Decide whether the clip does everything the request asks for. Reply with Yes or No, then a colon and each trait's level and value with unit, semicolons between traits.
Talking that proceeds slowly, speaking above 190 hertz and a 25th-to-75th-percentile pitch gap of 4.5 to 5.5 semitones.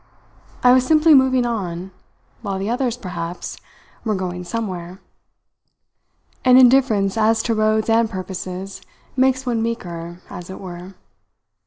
Yes: slow, 130 wpm; high, 215 Hz; average, 4.9 semitones